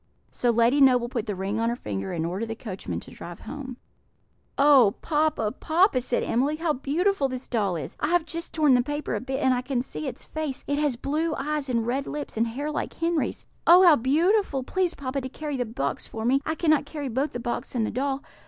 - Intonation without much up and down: No, average, 4.3 semitones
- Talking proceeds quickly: Yes, fast, 230 wpm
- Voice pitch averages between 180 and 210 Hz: No, very high, 270 Hz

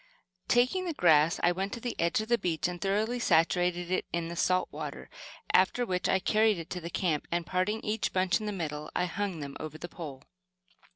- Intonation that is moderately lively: Yes, average, 3.9 semitones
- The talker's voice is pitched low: No, medium, 180 Hz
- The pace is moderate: No, fast, 220 wpm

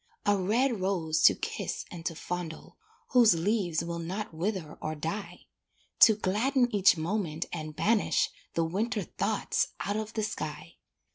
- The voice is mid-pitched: No, high, 195 Hz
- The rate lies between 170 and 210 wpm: No, average, 150 wpm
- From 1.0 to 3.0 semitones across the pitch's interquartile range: No, average, 4.5 semitones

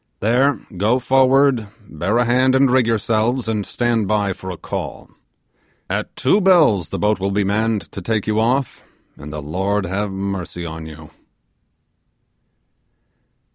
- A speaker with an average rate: Yes, average, 150 wpm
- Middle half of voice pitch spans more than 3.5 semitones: Yes, average, 4.4 semitones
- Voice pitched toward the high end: No, low, 110 Hz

